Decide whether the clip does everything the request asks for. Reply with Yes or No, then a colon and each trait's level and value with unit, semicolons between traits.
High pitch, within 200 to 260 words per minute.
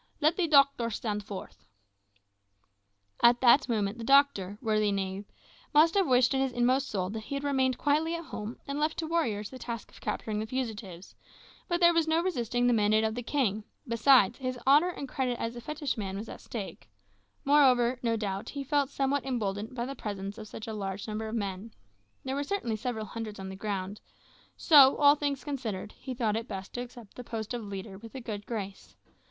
Yes: high, 235 Hz; fast, 205 wpm